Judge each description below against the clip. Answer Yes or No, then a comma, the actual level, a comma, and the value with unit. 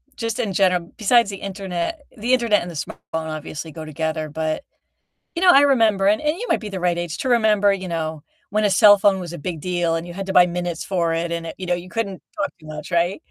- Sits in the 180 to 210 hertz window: Yes, medium, 185 Hz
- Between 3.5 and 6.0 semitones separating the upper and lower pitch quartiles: Yes, average, 3.9 semitones